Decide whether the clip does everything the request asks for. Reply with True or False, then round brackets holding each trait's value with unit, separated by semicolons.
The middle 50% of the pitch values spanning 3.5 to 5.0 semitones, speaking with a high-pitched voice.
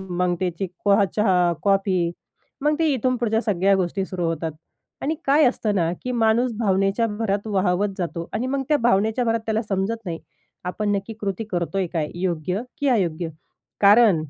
True (3.8 semitones; 200 Hz)